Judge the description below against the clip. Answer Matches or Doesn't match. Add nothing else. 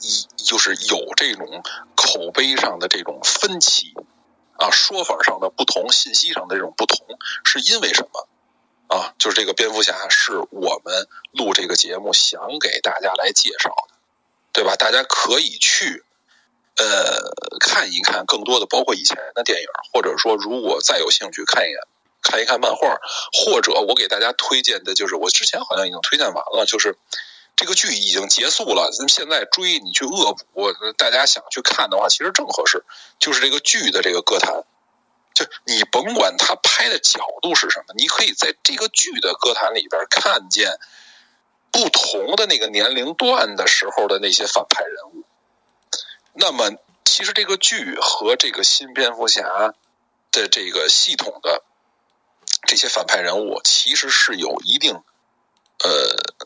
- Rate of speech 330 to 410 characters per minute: Doesn't match